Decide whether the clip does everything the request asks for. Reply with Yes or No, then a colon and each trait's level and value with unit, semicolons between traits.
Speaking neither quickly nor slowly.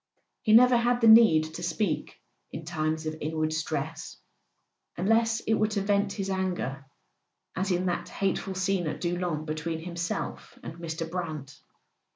Yes: average, 150 wpm